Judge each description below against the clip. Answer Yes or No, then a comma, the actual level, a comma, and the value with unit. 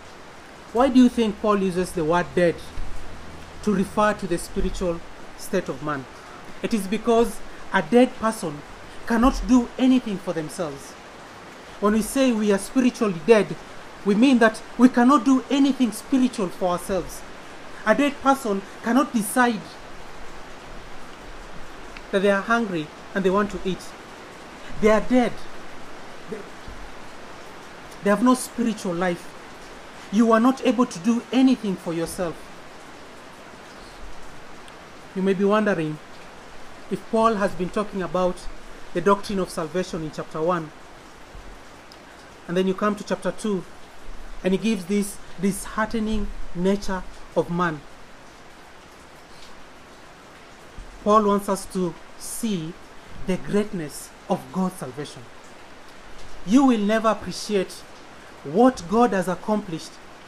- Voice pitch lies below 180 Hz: No, high, 200 Hz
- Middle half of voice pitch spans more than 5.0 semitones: No, average, 4.1 semitones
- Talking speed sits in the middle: No, slow, 125 wpm